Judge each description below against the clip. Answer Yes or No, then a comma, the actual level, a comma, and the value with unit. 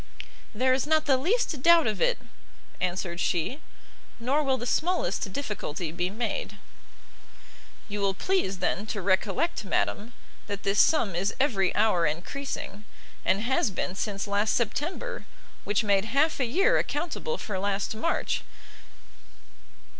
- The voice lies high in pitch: Yes, high, 215 Hz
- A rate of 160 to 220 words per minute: No, average, 140 wpm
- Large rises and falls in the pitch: Yes, wide, 6.8 semitones